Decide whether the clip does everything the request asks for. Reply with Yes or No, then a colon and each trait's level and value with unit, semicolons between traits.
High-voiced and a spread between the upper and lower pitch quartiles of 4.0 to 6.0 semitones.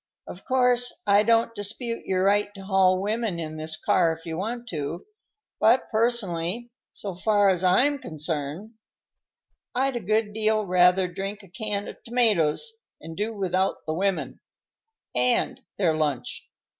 Yes: high, 200 Hz; average, 4.5 semitones